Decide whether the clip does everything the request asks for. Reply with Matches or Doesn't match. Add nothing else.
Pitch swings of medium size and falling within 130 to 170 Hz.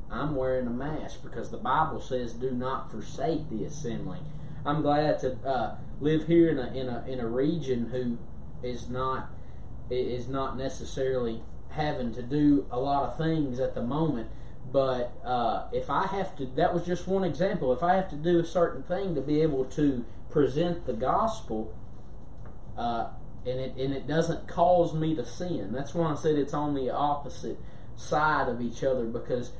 Matches